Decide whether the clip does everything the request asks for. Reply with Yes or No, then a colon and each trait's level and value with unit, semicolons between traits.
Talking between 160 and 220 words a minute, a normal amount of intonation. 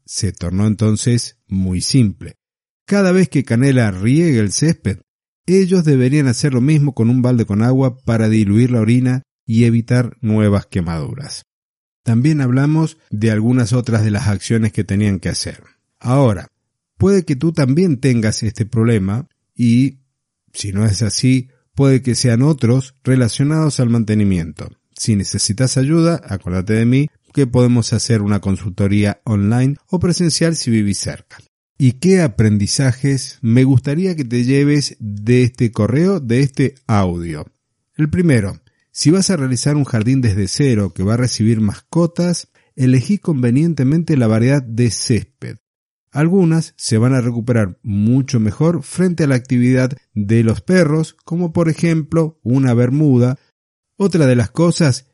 No: average, 150 wpm; average, 4.7 semitones